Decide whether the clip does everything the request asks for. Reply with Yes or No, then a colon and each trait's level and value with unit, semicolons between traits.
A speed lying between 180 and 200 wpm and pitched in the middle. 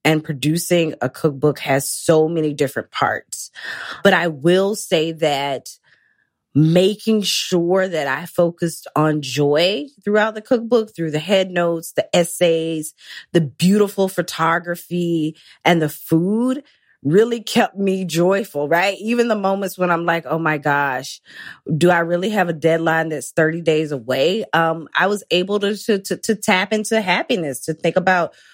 No: average, 155 wpm; medium, 170 Hz